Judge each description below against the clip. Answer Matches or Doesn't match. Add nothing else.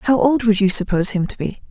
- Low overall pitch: Doesn't match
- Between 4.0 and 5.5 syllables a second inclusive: Doesn't match